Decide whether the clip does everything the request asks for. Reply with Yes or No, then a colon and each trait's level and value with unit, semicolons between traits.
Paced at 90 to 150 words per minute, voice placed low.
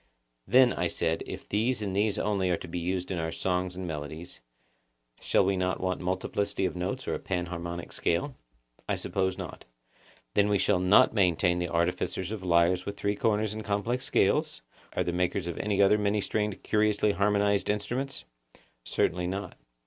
No: average, 180 wpm; very low, 95 Hz